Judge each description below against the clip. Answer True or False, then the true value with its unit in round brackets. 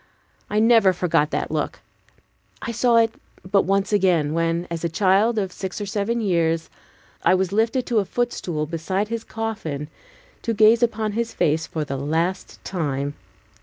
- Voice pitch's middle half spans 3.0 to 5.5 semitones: True (5.0 semitones)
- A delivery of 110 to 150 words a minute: False (165 wpm)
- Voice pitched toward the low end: False (190 Hz)